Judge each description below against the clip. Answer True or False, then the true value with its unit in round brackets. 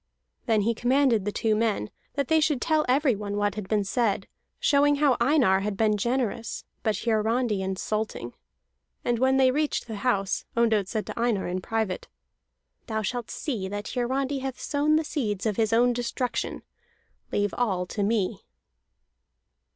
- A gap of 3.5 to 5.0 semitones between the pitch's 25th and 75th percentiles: True (4.0 semitones)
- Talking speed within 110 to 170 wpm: True (160 wpm)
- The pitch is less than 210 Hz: False (225 Hz)